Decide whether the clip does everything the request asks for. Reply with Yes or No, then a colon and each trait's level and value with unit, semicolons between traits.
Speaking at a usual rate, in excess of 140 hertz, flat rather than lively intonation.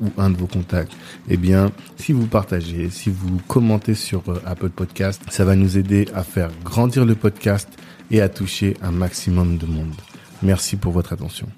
No: average, 185 wpm; very low, 95 Hz; narrow, 2.3 semitones